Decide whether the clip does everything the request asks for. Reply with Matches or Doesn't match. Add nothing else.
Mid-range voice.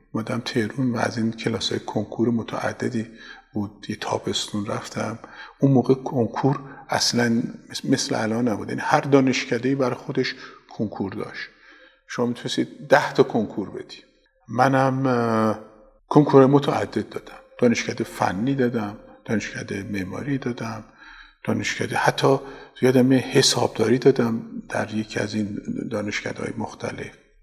Doesn't match